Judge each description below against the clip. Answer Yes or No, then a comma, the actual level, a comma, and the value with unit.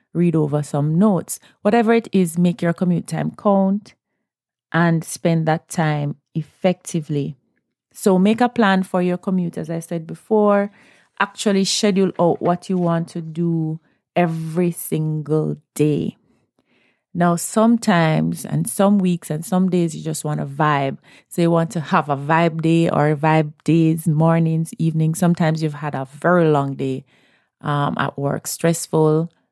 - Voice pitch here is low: No, medium, 165 Hz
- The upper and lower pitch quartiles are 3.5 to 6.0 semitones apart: No, average, 2.9 semitones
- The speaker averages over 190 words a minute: No, average, 155 wpm